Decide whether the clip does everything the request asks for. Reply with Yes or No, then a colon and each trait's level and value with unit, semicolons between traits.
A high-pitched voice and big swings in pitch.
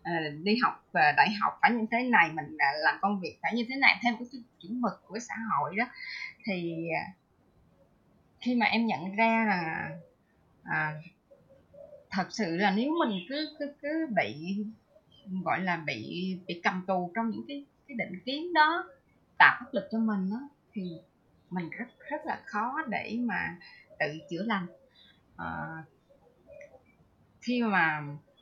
Yes: high, 215 Hz; wide, 5.8 semitones